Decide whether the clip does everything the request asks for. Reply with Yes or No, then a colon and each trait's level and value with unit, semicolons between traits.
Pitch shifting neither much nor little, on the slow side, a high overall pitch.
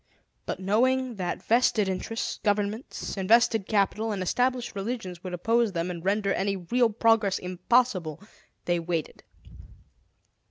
Yes: average, 3.9 semitones; slow, 125 wpm; high, 205 Hz